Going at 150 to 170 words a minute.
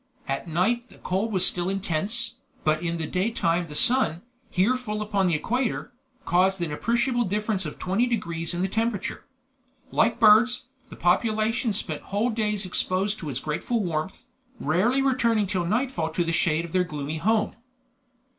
Yes: average, 165 wpm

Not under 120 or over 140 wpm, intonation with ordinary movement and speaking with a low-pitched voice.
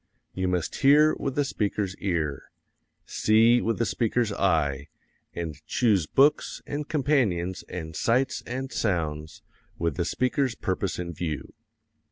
No: slow, 135 wpm; wide, 7.2 semitones; low, 100 Hz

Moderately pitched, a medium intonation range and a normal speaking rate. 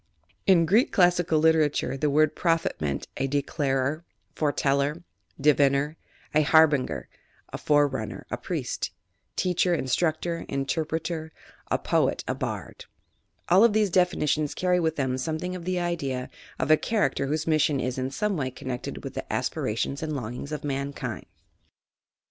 Yes: medium, 155 Hz; average, 3.6 semitones; average, 145 wpm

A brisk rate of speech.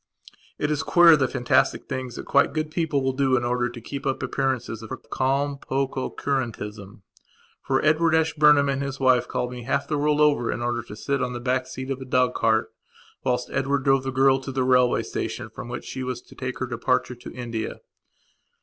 Yes: fast, 210 wpm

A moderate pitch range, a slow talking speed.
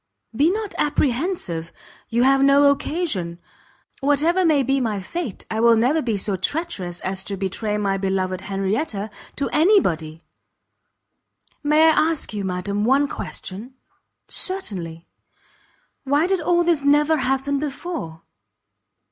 No: wide, 7.9 semitones; slow, 130 wpm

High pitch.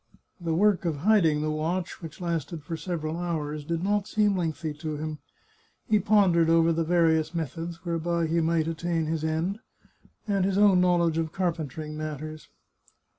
No: medium, 165 Hz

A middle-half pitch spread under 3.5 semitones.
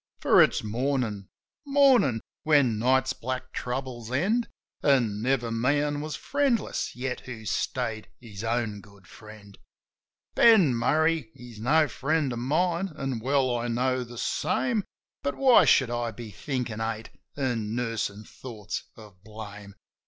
No: average, 4.3 semitones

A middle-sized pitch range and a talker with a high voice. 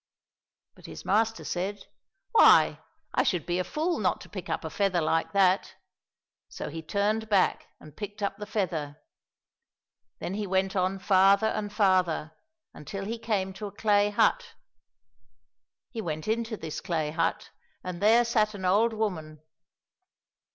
Yes: average, 3.3 semitones; high, 195 Hz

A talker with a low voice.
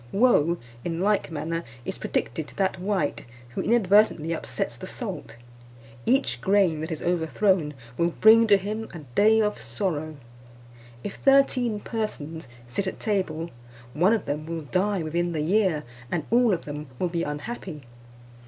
No: medium, 180 Hz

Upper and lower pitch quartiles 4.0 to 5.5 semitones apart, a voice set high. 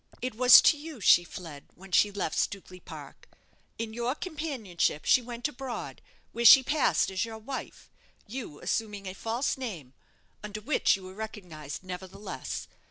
Yes: average, 5.2 semitones; high, 220 Hz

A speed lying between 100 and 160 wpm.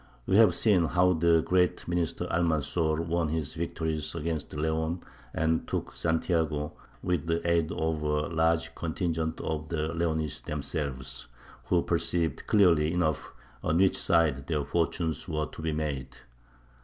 Yes: average, 145 wpm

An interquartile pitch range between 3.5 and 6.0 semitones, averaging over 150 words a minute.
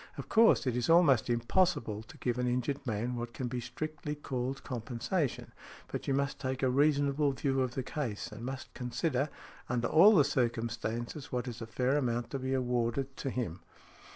No: average, 2.8 semitones; average, 190 wpm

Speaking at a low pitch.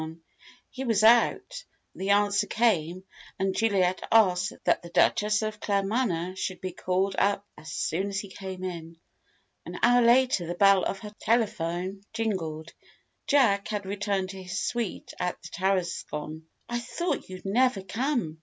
No: high, 195 Hz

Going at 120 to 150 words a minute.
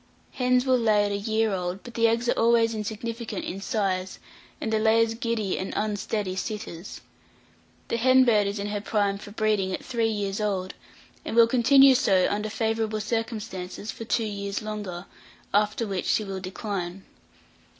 No: average, 170 wpm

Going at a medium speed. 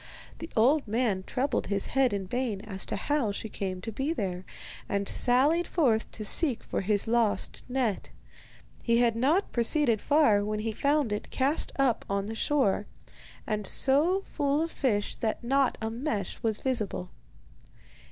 Yes: average, 160 wpm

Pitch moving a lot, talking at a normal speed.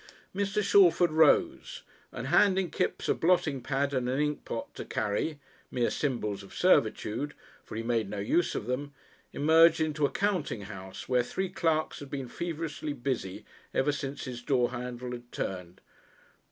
No: average, 5.0 semitones; average, 160 wpm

